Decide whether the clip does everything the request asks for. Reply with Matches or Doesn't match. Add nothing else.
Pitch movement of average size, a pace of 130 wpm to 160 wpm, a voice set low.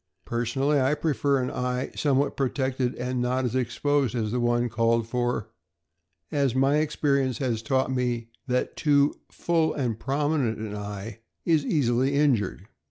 Matches